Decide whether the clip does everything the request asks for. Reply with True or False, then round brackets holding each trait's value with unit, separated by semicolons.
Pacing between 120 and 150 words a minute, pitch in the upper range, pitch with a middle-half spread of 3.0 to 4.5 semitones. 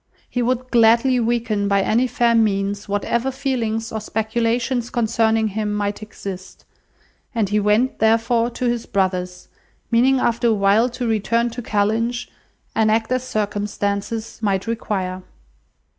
False (140 wpm; 225 Hz; 2.5 semitones)